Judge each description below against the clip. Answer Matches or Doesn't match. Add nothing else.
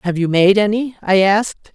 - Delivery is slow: Doesn't match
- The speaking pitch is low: Doesn't match